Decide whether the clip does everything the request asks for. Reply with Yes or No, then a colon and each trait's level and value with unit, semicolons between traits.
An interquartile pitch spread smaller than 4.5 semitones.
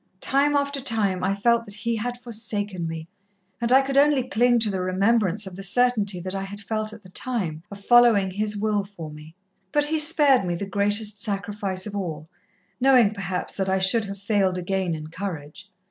Yes: average, 3.7 semitones